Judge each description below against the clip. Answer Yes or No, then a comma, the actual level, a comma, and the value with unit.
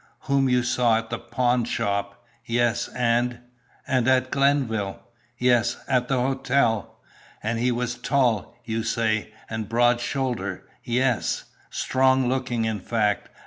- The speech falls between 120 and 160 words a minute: Yes, slow, 135 wpm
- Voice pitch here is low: Yes, low, 120 Hz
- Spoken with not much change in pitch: Yes, narrow, 2.2 semitones